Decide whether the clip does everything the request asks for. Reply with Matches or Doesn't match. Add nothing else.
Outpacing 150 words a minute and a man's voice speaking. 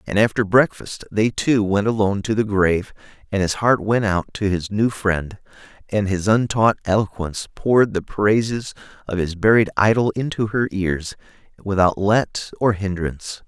Matches